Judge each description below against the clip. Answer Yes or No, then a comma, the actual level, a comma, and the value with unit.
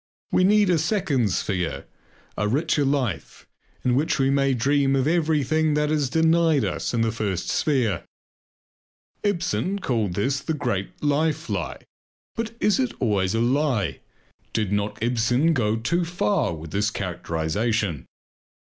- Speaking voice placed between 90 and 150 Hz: Yes, low, 135 Hz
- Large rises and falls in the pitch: Yes, wide, 7.0 semitones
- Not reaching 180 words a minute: Yes, average, 145 wpm